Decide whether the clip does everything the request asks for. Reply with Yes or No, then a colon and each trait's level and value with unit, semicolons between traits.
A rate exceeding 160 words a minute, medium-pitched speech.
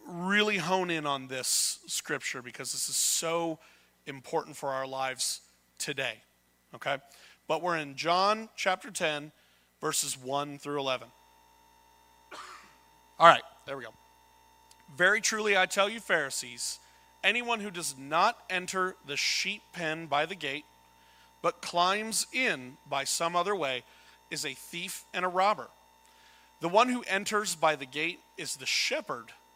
No: average, 145 wpm; medium, 145 Hz